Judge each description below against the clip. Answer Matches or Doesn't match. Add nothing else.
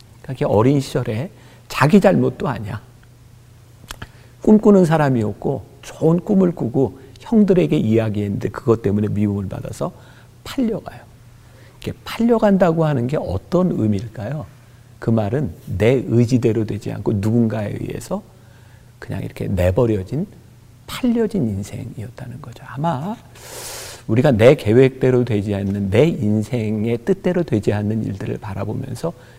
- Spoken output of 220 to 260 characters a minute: Doesn't match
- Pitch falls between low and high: Doesn't match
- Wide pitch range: Doesn't match